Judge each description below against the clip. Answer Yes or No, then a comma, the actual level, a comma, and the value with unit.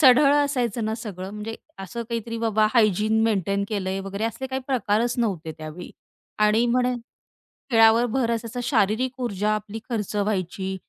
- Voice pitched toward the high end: Yes, high, 220 Hz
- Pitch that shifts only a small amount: No, average, 3.1 semitones